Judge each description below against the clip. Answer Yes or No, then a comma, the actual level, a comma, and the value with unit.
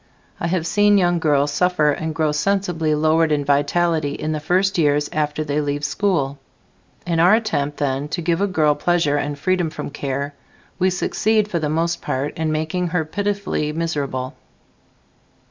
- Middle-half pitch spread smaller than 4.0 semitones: Yes, average, 3.4 semitones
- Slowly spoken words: No, average, 170 wpm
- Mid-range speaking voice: Yes, medium, 155 Hz